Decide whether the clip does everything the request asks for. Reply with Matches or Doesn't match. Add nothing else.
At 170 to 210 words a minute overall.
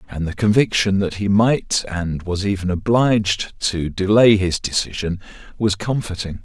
Doesn't match